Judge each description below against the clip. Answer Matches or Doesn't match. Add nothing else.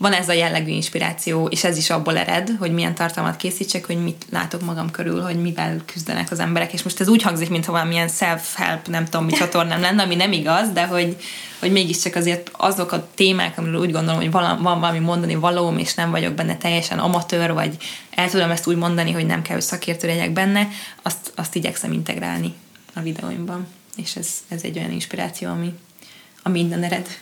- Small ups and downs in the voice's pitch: Matches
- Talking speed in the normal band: Doesn't match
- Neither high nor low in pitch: Matches